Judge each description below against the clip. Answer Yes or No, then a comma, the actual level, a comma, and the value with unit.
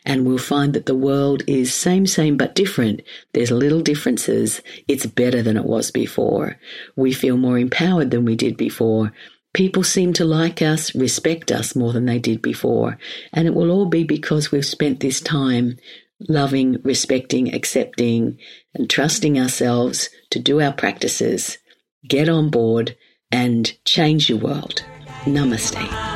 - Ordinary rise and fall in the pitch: Yes, average, 4.3 semitones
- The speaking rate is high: No, average, 155 wpm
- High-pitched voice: No, low, 135 Hz